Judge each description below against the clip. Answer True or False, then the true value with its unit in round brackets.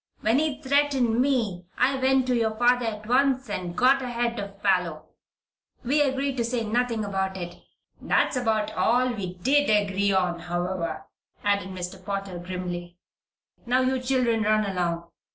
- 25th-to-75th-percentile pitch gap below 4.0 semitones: False (5.2 semitones)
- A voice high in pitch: True (220 Hz)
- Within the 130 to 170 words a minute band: True (155 wpm)